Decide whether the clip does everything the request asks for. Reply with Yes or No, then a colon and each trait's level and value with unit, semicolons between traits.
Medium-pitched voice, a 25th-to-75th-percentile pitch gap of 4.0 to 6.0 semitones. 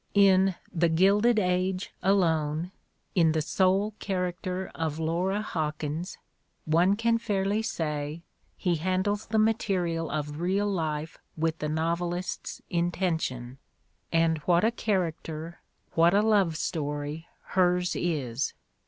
No: medium, 175 Hz; average, 3.2 semitones